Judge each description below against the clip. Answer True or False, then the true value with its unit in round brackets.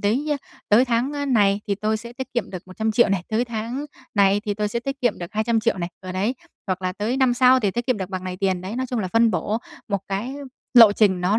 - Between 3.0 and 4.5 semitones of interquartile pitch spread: True (3.6 semitones)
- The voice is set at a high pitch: True (215 Hz)